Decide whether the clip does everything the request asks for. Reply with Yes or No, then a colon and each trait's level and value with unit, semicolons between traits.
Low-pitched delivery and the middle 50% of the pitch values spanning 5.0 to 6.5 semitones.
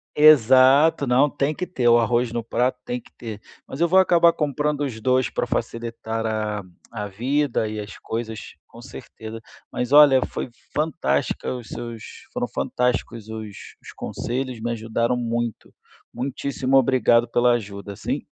No: low, 120 Hz; average, 3.4 semitones